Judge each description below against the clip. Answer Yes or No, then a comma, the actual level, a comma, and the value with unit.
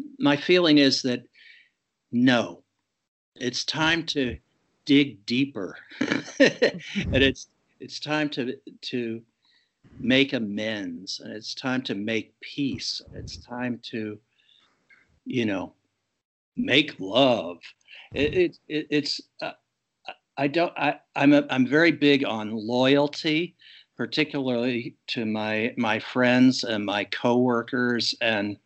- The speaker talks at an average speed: No, slow, 115 wpm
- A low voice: Yes, low, 130 Hz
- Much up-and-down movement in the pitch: No, average, 4.4 semitones